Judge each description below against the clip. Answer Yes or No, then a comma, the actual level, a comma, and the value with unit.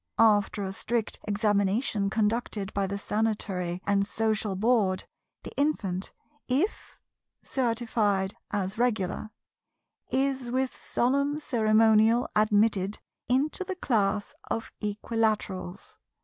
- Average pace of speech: No, slow, 100 wpm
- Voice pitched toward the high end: Yes, high, 215 Hz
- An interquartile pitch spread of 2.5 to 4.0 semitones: Yes, average, 3.1 semitones